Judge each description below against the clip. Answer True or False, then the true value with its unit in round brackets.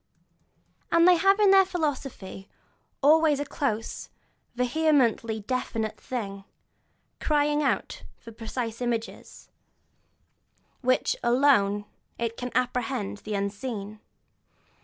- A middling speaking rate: False (95 wpm)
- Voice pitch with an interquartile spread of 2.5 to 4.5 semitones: False (5.2 semitones)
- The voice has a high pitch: True (250 Hz)